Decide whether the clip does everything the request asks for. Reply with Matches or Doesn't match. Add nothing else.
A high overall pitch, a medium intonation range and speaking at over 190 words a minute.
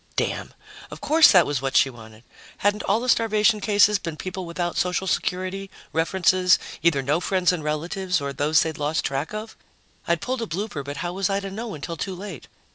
Doesn't match